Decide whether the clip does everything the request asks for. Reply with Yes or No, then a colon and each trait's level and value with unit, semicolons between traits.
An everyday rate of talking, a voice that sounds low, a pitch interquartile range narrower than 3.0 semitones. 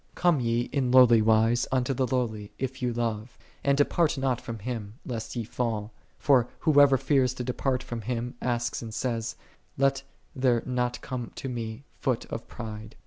Yes: average, 180 wpm; low, 125 Hz; narrow, 2.4 semitones